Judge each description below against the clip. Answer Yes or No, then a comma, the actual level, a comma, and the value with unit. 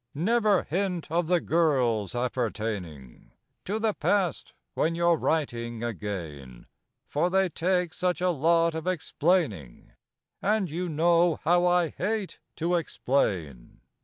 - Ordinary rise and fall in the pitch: No, wide, 7.2 semitones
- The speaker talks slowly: Yes, slow, 125 wpm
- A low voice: No, medium, 165 Hz